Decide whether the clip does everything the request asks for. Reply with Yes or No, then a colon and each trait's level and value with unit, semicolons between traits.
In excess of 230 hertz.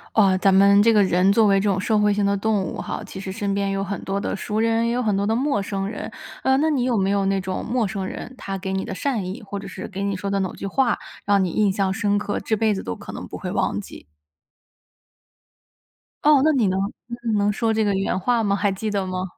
No: high, 200 Hz